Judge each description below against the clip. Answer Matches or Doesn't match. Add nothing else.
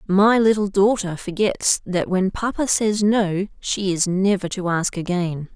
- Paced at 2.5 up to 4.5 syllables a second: Matches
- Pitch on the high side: Matches